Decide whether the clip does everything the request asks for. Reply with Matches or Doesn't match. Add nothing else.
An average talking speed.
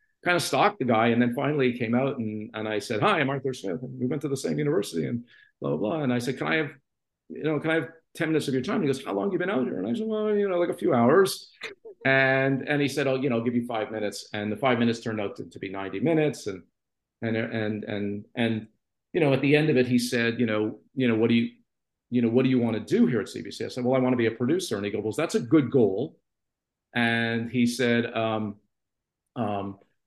Doesn't match